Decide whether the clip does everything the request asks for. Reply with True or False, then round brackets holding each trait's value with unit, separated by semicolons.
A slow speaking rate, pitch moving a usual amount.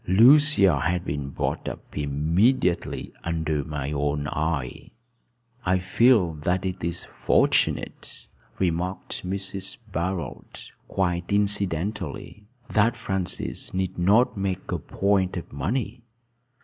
True (110 wpm; 3.7 semitones)